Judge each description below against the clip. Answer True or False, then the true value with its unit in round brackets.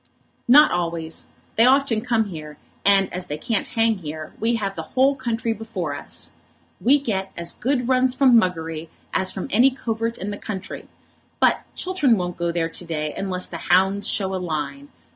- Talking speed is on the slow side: False (180 wpm)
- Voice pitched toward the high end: True (200 Hz)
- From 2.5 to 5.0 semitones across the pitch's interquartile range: False (5.6 semitones)